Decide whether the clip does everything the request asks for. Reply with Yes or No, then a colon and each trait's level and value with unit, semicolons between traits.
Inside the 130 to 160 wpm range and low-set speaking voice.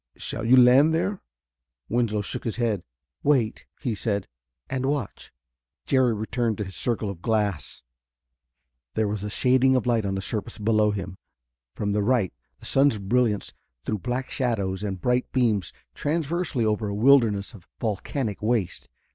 Yes: average, 155 wpm; low, 110 Hz